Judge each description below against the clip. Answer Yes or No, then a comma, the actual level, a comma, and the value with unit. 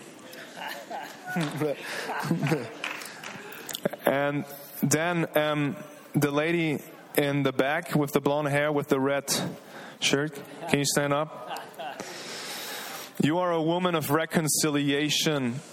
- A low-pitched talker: No, medium, 150 Hz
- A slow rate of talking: Yes, slow, 100 wpm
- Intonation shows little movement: Yes, narrow, 1.9 semitones